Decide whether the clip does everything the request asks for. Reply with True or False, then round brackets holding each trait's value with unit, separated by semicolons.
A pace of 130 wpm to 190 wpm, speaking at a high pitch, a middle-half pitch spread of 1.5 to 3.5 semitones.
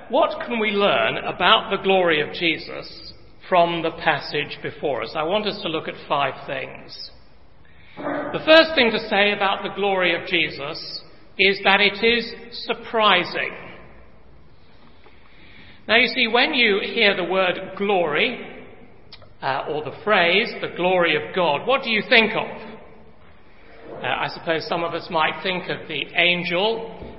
False (155 wpm; 195 Hz; 4.8 semitones)